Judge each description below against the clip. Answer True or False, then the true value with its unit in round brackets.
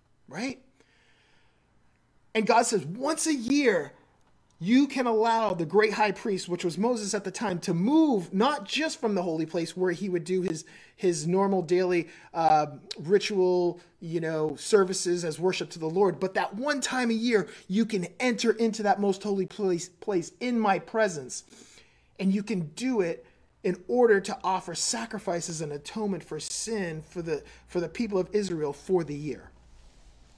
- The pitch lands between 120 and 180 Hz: False (190 Hz)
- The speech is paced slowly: False (175 wpm)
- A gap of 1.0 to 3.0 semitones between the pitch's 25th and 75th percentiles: False (4.3 semitones)